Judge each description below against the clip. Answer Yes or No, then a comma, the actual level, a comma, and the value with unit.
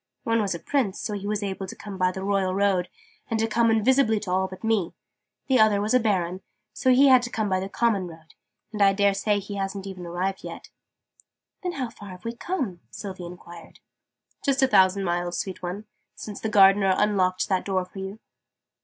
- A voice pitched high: Yes, high, 200 Hz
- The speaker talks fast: Yes, fast, 215 wpm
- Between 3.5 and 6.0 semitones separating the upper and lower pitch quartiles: No, average, 2.9 semitones